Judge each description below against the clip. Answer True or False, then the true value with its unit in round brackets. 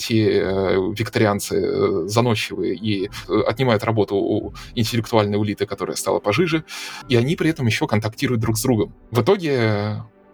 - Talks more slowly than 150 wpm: True (135 wpm)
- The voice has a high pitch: False (115 Hz)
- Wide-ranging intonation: False (3.4 semitones)